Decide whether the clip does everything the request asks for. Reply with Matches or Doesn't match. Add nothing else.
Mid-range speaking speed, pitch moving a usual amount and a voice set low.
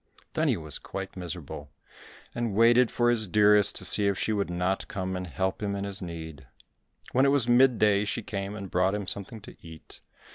Doesn't match